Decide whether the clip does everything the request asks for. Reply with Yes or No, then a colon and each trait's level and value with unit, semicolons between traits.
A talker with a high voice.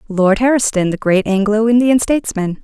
Yes: high, 215 Hz